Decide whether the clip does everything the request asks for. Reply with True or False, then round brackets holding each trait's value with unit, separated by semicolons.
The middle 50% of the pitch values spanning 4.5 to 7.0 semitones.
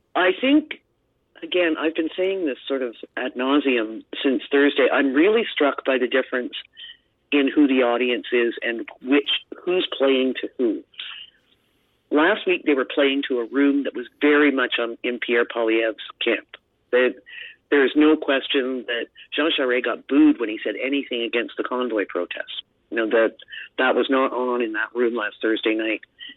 True (5.3 semitones)